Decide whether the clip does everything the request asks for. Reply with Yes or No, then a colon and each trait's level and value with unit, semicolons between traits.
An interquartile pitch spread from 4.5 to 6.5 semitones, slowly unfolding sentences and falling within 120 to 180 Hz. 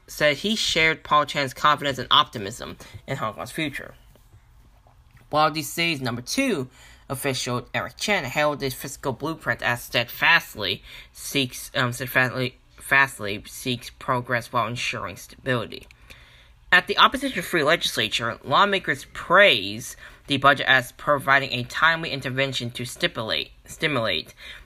No: average, 3.3 semitones; slow, 125 wpm; low, 135 Hz